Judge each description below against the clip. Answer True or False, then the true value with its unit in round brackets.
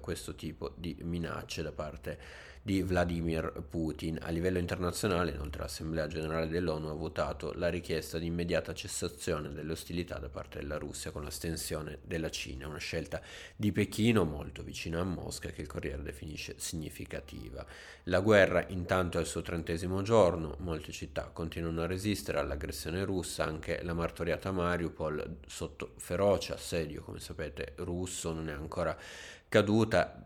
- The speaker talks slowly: False (150 wpm)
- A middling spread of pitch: False (2.1 semitones)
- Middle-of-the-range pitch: False (85 Hz)